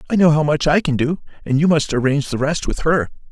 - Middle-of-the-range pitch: Yes, medium, 150 Hz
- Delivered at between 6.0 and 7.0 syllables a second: Yes, 6.3 syllables/s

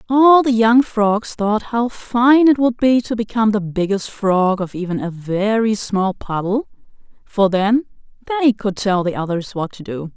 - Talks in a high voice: Yes, high, 215 Hz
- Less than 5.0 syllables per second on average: Yes, 4.3 syllables/s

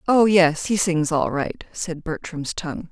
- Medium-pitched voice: Yes, medium, 170 Hz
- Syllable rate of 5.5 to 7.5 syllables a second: No, 4.2 syllables/s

